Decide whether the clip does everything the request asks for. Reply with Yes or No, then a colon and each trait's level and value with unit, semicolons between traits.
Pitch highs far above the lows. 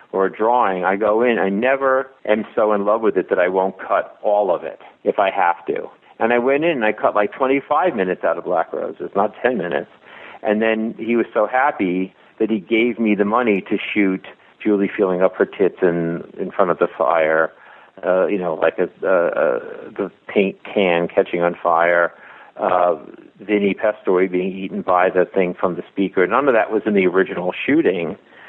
No: average, 3.1 semitones